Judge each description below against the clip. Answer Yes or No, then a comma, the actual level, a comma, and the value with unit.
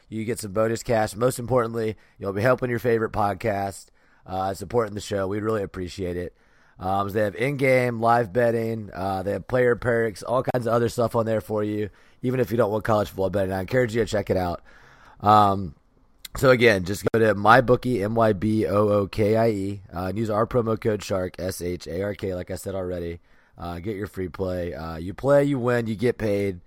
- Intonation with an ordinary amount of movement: Yes, average, 3.3 semitones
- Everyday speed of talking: No, fast, 225 wpm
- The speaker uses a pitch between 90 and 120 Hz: Yes, low, 105 Hz